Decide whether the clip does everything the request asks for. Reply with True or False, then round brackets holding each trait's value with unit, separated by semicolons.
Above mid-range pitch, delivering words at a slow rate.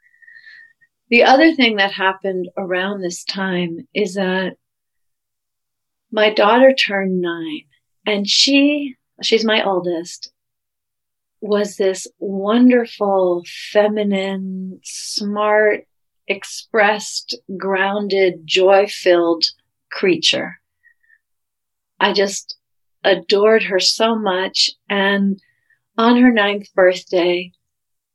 True (200 Hz; 85 wpm)